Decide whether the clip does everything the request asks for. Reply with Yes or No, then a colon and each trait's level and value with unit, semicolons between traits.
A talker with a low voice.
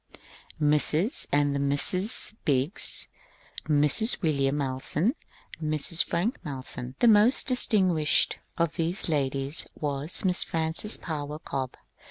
No: medium, 155 Hz